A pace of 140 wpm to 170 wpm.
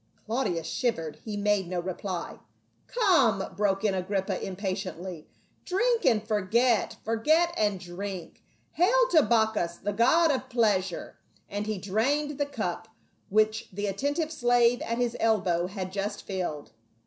Yes: average, 155 wpm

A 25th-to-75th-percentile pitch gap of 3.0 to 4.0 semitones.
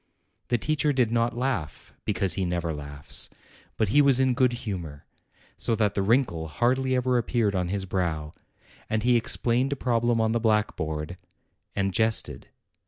No: average, 5.3 semitones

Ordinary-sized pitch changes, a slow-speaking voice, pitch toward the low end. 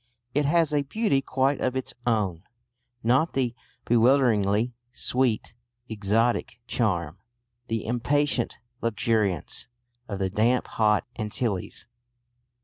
Yes: average, 3.8 semitones; slow, 105 wpm; low, 115 Hz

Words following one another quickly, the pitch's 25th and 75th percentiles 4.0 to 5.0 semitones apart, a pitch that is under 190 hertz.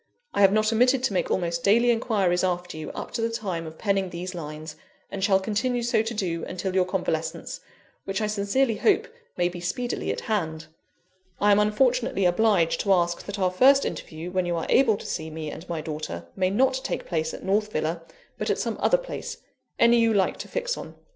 No: fast, 215 wpm; average, 4.7 semitones; high, 195 Hz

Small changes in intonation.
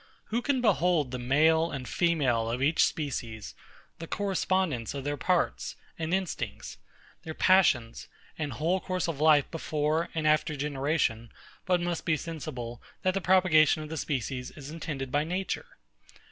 No: average, 4.4 semitones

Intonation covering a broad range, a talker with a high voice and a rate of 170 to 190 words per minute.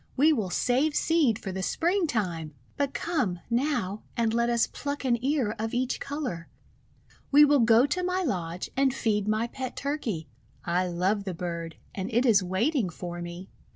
Yes: wide, 7.1 semitones; high, 230 Hz; average, 175 wpm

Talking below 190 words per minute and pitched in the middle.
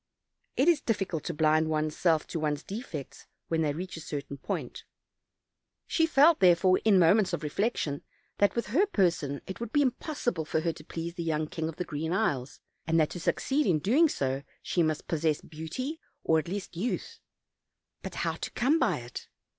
No: average, 195 wpm; medium, 170 Hz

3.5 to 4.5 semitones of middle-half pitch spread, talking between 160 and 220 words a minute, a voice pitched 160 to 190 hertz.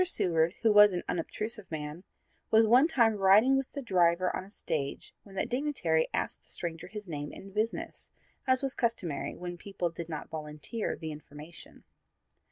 No: wide, 5.5 semitones; average, 175 wpm; medium, 185 Hz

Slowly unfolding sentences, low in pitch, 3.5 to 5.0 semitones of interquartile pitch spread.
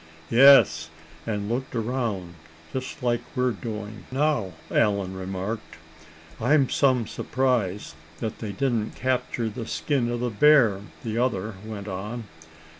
Yes: slow, 125 wpm; low, 115 Hz; average, 3.8 semitones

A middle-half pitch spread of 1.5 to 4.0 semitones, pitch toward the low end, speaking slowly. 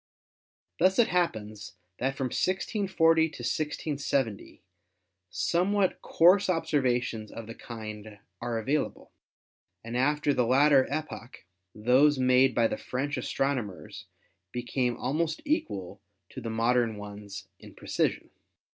No: average, 5.3 semitones; low, 130 Hz; slow, 120 wpm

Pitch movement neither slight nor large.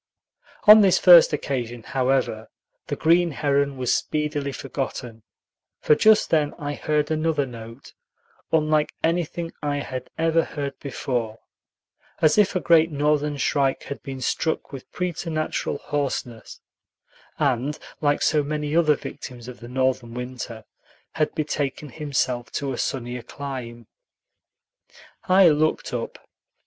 Yes: average, 3.3 semitones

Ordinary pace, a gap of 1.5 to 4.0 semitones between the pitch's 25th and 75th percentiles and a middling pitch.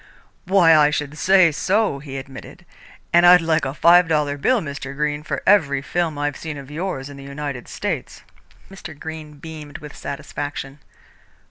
Yes: average, 165 wpm; average, 2.8 semitones; medium, 150 Hz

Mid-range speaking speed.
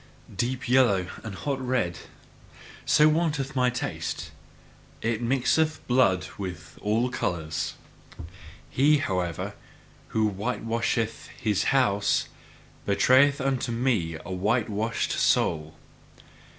No: slow, 100 wpm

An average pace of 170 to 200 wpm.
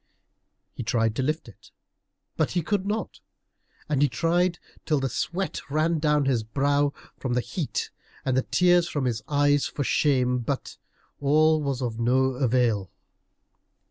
No: average, 155 wpm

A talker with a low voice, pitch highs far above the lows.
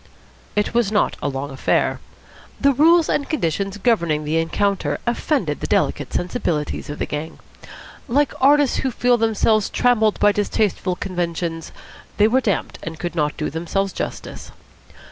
No: high, 200 Hz; wide, 6.6 semitones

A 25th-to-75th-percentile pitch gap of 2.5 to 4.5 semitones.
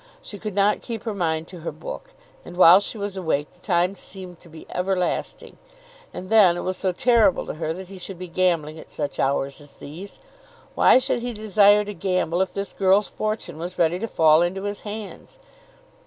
Yes: average, 3.2 semitones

